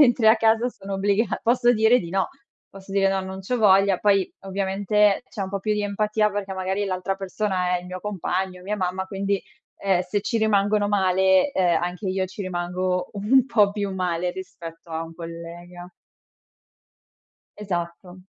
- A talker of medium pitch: No, high, 195 Hz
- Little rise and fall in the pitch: Yes, narrow, 2.2 semitones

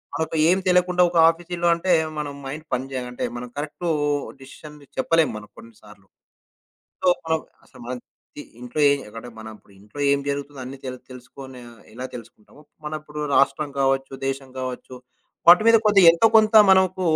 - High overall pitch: No, medium, 140 Hz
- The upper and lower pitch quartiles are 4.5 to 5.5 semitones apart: Yes, average, 4.8 semitones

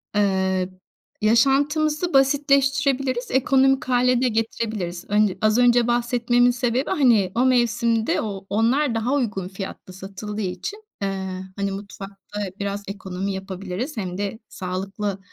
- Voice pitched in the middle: No, high, 225 Hz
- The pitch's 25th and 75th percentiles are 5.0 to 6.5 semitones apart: No, average, 4.6 semitones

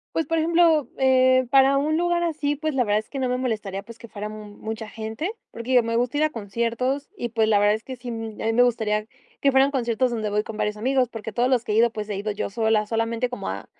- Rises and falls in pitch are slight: No, average, 3.5 semitones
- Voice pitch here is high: Yes, high, 235 Hz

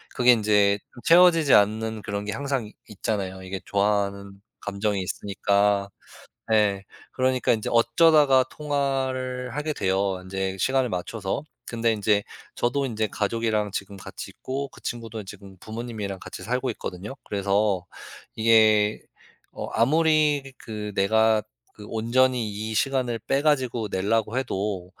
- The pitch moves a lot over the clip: No, average, 4.1 semitones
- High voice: No, low, 110 Hz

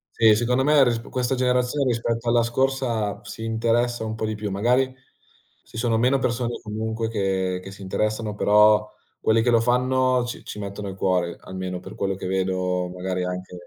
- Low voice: Yes, low, 110 Hz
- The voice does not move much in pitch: No, average, 3.9 semitones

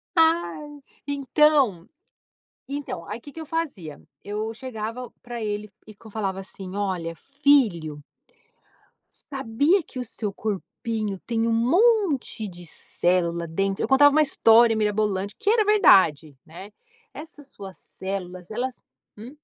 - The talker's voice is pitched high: Yes, high, 220 Hz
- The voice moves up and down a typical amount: No, wide, 6.6 semitones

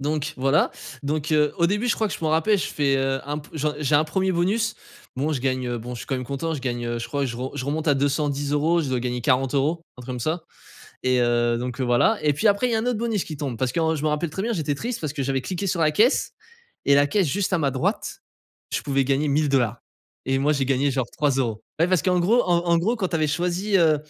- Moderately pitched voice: Yes, medium, 150 Hz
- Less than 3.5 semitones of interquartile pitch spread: No, average, 4.2 semitones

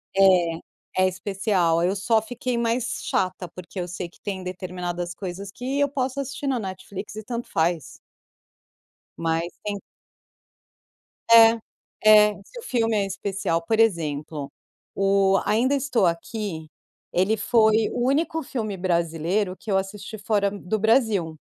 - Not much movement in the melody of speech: No, average, 4.1 semitones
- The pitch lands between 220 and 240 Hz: No, high, 195 Hz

